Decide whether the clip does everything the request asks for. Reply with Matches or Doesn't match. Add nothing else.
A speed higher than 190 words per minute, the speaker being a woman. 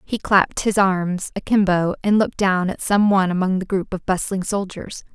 Matches